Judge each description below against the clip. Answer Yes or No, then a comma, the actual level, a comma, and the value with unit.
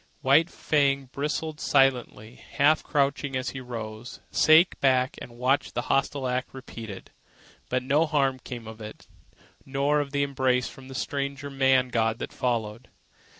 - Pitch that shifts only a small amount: Yes, narrow, 2.1 semitones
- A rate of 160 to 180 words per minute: No, average, 150 wpm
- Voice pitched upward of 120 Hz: Yes, low, 135 Hz